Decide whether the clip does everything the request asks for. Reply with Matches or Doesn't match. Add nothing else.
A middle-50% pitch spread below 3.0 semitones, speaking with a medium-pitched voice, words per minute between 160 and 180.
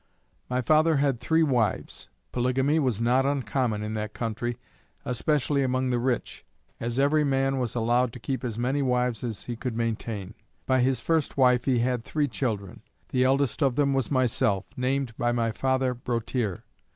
Doesn't match